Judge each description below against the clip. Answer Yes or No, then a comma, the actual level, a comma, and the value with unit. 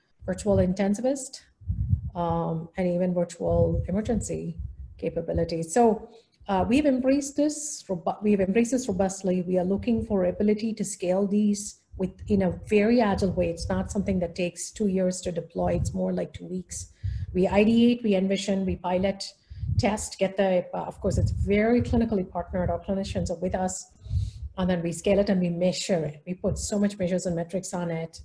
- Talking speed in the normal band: Yes, average, 180 wpm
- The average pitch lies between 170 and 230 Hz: Yes, medium, 185 Hz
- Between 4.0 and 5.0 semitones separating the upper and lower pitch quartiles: No, average, 3.4 semitones